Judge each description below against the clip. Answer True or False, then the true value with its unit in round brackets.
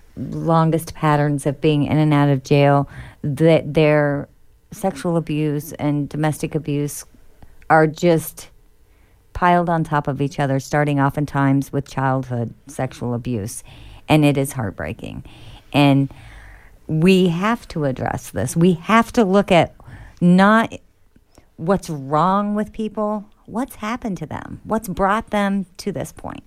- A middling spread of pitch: True (4.6 semitones)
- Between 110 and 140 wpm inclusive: True (135 wpm)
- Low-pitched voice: False (150 Hz)